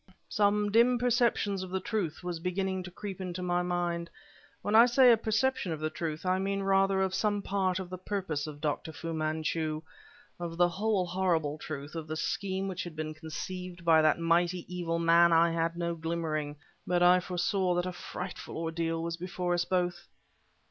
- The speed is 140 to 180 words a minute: No, average, 190 wpm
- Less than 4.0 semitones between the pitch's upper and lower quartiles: Yes, narrow, 2.5 semitones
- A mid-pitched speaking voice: Yes, medium, 175 Hz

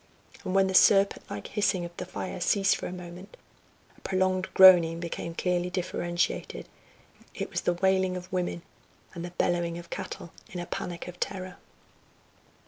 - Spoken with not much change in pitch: Yes, narrow, 1.4 semitones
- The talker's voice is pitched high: No, medium, 180 Hz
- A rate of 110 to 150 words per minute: No, average, 165 wpm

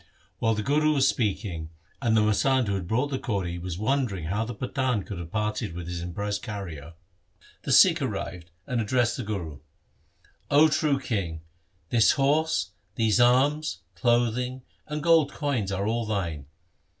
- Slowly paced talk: No, average, 170 wpm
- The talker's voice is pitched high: No, low, 110 Hz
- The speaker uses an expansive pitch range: Yes, wide, 5.7 semitones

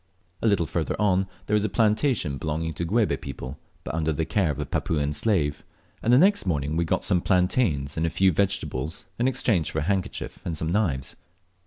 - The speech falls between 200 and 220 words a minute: Yes, fast, 205 wpm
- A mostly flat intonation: No, average, 5.3 semitones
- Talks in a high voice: No, very low, 85 Hz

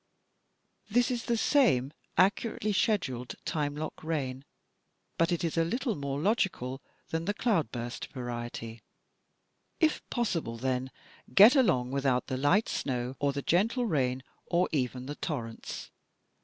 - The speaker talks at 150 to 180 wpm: No, slow, 135 wpm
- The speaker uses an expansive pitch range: Yes, wide, 8.1 semitones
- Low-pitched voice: No, medium, 145 Hz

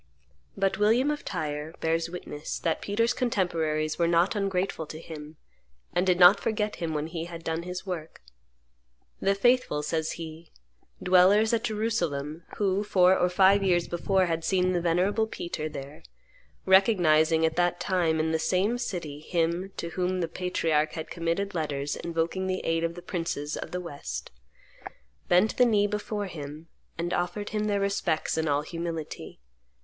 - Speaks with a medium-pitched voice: Yes, medium, 175 Hz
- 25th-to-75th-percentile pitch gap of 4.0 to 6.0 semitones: No, average, 3.4 semitones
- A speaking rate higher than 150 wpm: Yes, average, 165 wpm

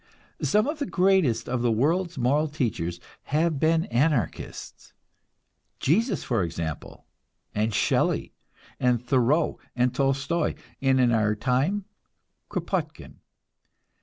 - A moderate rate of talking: No, slow, 110 wpm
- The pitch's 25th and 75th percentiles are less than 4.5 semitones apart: No, wide, 5.6 semitones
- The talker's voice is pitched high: No, low, 135 Hz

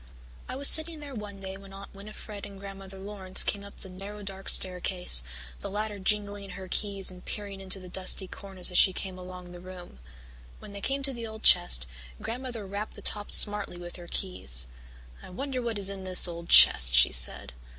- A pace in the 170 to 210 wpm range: Yes, average, 200 wpm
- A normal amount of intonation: No, narrow, 2.2 semitones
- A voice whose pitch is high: Yes, high, 195 Hz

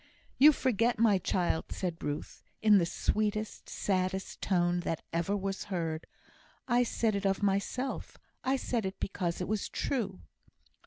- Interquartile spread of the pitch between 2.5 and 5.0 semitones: Yes, average, 3.6 semitones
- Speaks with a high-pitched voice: Yes, high, 195 Hz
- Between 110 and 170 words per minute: Yes, average, 150 wpm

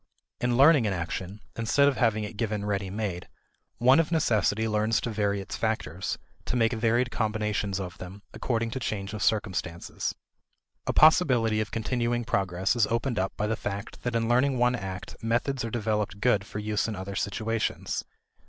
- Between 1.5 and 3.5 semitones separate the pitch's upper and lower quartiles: Yes, average, 2.9 semitones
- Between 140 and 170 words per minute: No, average, 180 wpm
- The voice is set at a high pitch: No, low, 110 Hz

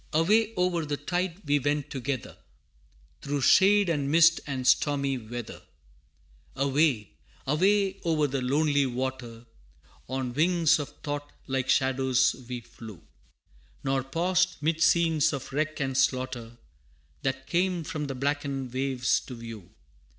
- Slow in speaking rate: Yes, slow, 130 wpm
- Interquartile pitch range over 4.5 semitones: No, average, 3.5 semitones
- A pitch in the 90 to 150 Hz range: Yes, medium, 140 Hz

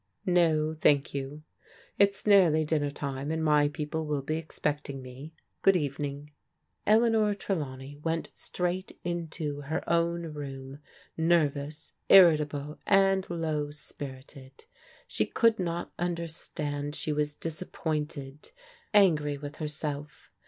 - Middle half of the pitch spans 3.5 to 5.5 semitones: No, average, 2.8 semitones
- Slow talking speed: Yes, slow, 115 wpm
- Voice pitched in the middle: Yes, medium, 150 Hz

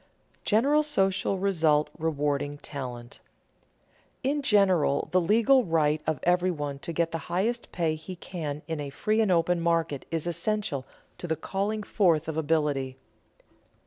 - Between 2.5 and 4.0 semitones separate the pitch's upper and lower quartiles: No, average, 4.8 semitones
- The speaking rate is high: No, average, 150 wpm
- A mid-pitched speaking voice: Yes, medium, 165 Hz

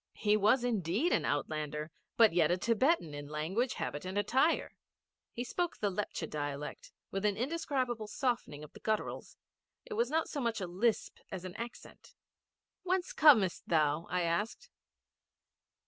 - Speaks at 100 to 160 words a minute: Yes, average, 155 wpm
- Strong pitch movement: Yes, wide, 6.8 semitones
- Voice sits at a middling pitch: No, high, 210 Hz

